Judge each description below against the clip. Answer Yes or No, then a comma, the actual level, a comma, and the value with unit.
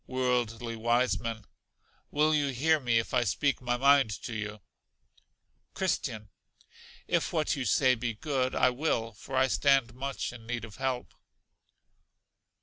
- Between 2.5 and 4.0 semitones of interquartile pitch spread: Yes, average, 2.9 semitones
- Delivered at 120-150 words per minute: Yes, average, 145 wpm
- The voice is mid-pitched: No, low, 125 Hz